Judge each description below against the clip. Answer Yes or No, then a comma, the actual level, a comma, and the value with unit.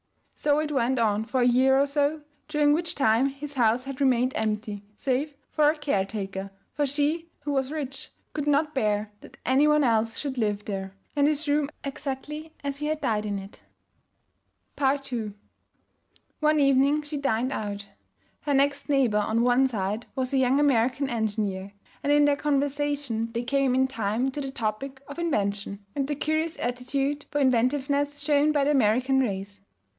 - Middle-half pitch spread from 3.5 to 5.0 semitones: Yes, average, 4.4 semitones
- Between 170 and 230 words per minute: Yes, average, 175 wpm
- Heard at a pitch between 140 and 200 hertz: No, very high, 270 Hz